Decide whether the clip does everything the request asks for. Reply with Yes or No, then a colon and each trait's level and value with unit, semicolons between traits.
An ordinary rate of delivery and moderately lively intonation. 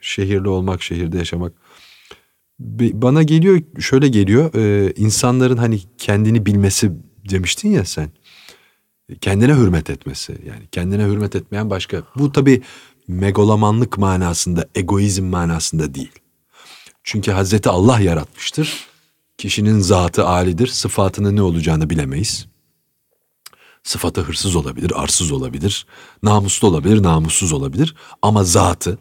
Yes: average, 110 wpm; average, 4.4 semitones